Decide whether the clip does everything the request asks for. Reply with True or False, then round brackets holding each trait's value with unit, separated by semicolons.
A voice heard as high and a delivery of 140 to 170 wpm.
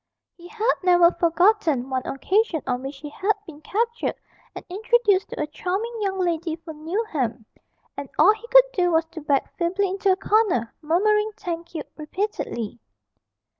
True (355 Hz; 165 wpm)